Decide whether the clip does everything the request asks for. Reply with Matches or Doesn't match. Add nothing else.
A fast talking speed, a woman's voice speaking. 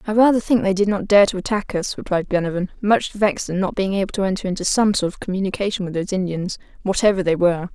Matches